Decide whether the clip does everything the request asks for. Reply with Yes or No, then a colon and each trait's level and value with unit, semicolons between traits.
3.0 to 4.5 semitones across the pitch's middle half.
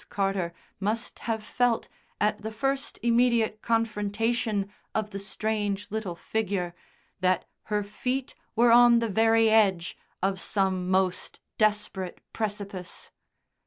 No: narrow, 2.6 semitones